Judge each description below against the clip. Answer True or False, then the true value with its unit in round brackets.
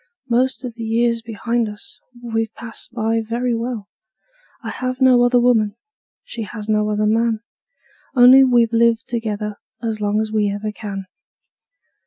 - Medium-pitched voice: False (230 Hz)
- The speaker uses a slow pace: False (155 wpm)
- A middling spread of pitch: False (2.0 semitones)